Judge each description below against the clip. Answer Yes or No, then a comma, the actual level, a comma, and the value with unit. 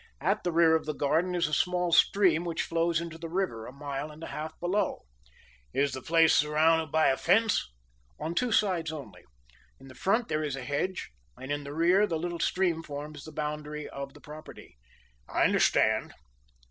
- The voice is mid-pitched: Yes, medium, 160 Hz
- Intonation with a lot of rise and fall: No, average, 2.9 semitones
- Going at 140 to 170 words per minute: No, average, 195 wpm